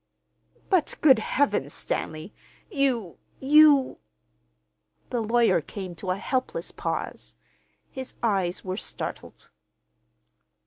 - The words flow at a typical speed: No, slow, 90 wpm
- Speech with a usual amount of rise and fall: No, wide, 6.5 semitones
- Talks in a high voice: Yes, high, 230 Hz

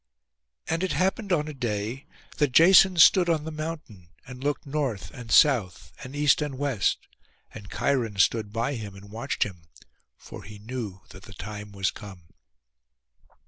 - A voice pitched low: Yes, low, 125 Hz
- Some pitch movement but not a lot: No, wide, 6.5 semitones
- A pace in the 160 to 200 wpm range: Yes, average, 165 wpm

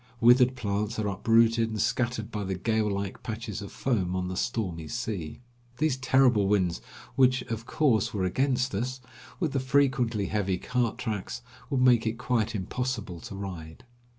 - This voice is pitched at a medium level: No, low, 115 Hz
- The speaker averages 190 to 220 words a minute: No, average, 165 wpm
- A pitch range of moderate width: Yes, average, 4.1 semitones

